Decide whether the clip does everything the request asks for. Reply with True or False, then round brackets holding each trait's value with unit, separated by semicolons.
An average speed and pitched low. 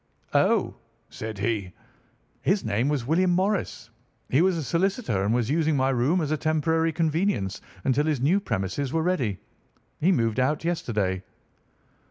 False (155 wpm; 145 Hz)